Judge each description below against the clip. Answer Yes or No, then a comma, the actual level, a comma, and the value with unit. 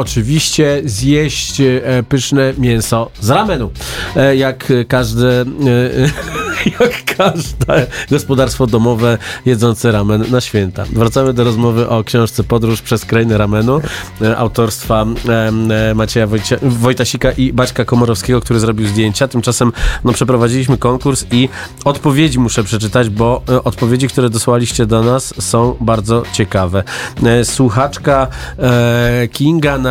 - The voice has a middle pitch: No, low, 120 Hz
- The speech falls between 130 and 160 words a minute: No, slow, 110 wpm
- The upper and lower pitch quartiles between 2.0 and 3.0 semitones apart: Yes, narrow, 2.5 semitones